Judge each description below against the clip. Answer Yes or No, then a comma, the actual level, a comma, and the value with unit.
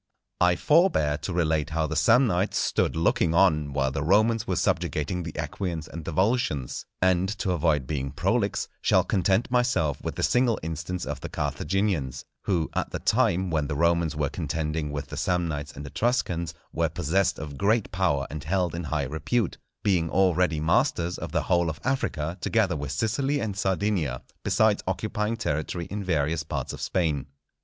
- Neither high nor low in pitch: No, very low, 85 Hz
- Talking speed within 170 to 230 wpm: Yes, average, 175 wpm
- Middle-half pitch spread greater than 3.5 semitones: Yes, average, 4.2 semitones